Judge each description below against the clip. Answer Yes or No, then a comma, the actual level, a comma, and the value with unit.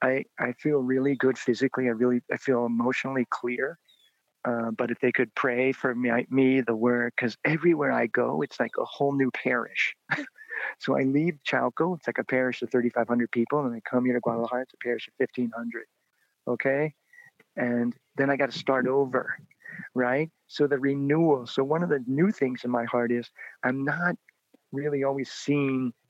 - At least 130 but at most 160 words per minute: No, average, 190 wpm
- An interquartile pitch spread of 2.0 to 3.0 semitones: Yes, narrow, 2.5 semitones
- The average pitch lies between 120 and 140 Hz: Yes, low, 130 Hz